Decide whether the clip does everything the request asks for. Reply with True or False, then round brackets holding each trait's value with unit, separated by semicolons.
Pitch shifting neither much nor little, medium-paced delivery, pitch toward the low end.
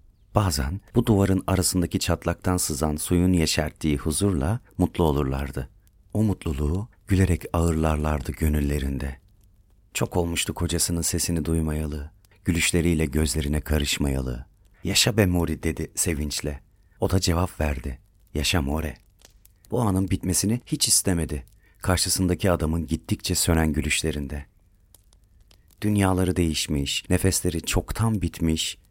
True (3.7 semitones; 105 wpm; 85 Hz)